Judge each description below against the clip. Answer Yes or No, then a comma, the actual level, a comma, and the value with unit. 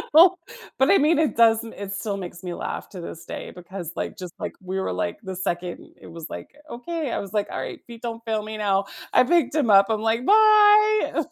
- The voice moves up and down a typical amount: No, wide, 7.7 semitones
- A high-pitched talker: Yes, high, 215 Hz